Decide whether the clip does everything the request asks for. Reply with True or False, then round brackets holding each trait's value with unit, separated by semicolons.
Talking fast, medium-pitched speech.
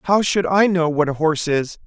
True (255 wpm; 170 Hz)